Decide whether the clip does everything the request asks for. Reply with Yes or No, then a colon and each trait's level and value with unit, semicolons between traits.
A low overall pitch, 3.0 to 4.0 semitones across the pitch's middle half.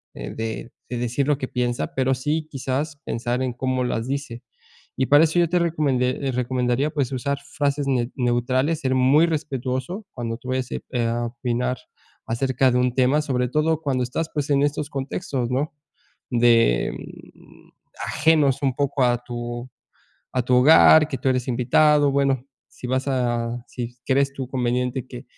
No: low, 130 Hz; narrow, 2.6 semitones